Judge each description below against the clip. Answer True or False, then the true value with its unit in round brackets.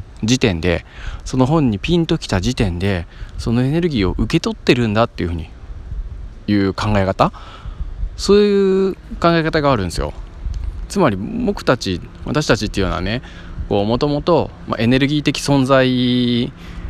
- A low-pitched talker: True (110 Hz)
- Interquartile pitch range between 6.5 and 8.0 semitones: True (7.5 semitones)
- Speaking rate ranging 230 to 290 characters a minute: False (300 characters per minute)